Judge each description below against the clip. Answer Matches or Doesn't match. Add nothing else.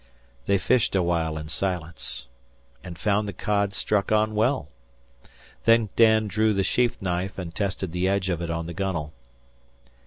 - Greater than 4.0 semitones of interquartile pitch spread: Doesn't match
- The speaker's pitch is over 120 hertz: Doesn't match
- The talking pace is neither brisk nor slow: Matches